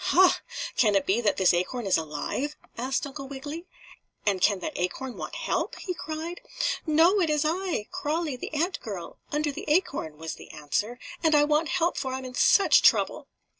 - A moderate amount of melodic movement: No, wide, 7.4 semitones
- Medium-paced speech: Yes, average, 190 wpm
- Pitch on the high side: Yes, very high, 285 Hz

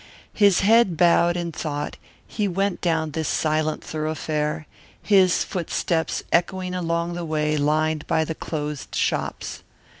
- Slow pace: Yes, slow, 130 wpm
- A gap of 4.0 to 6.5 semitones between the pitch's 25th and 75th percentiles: No, narrow, 2.4 semitones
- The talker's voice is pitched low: No, medium, 165 Hz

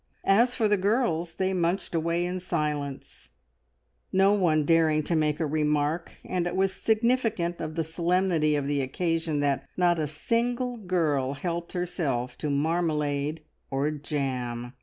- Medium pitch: Yes, medium, 165 Hz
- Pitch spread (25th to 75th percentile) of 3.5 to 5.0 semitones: Yes, average, 3.8 semitones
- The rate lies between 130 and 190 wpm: Yes, average, 150 wpm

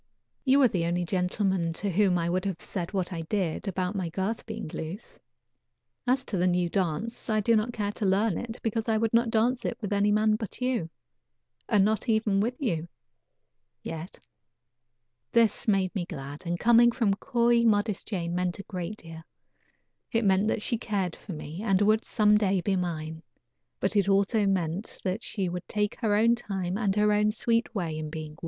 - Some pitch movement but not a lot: Yes, average, 3.6 semitones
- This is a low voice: No, high, 200 Hz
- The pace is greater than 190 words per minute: Yes, average, 200 wpm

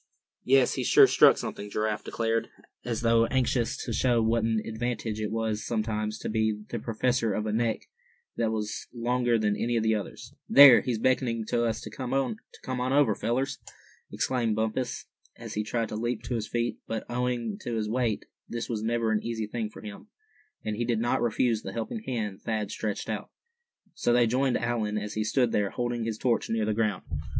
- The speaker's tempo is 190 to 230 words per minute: Yes, average, 200 wpm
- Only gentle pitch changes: Yes, narrow, 1.9 semitones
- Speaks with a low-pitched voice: Yes, low, 115 Hz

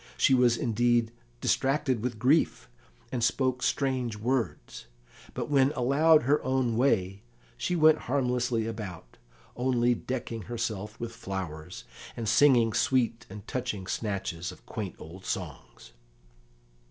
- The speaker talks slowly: Yes, slow, 125 wpm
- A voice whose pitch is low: Yes, low, 120 Hz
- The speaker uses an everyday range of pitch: Yes, average, 3.8 semitones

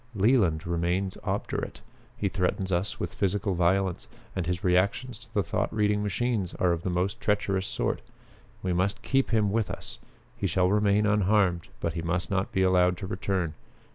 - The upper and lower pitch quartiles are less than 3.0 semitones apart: Yes, narrow, 2.6 semitones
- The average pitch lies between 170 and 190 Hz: No, very low, 95 Hz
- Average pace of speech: Yes, average, 175 wpm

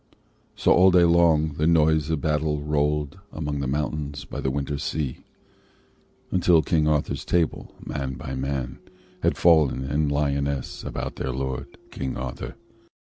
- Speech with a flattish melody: Yes, narrow, 2.3 semitones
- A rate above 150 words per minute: No, average, 145 wpm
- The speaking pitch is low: Yes, very low, 75 Hz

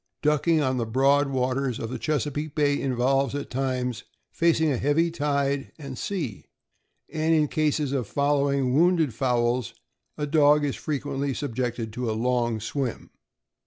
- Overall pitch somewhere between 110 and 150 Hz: Yes, medium, 140 Hz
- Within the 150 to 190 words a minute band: Yes, average, 155 wpm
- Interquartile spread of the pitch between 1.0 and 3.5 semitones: Yes, average, 2.9 semitones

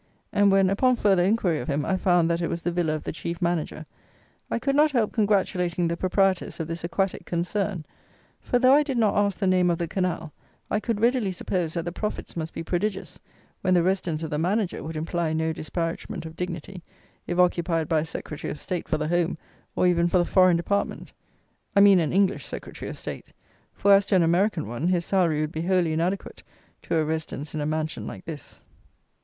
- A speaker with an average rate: No, fast, 215 wpm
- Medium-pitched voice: Yes, medium, 175 Hz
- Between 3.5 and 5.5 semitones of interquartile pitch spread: No, average, 3.0 semitones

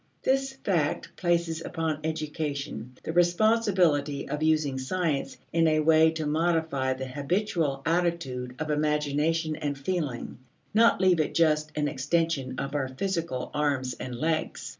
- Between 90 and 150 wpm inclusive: Yes, average, 140 wpm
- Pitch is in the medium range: Yes, medium, 155 Hz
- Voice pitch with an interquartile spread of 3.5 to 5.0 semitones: No, average, 3.1 semitones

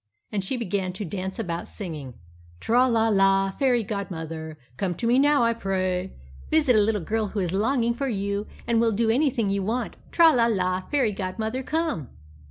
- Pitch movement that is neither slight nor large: Yes, average, 4.0 semitones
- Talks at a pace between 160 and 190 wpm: Yes, average, 185 wpm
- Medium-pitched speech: No, high, 210 Hz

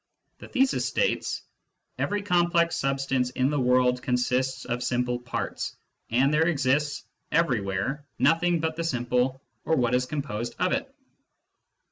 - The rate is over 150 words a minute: No, average, 140 wpm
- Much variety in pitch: No, average, 4.5 semitones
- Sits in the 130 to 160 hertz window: Yes, low, 135 Hz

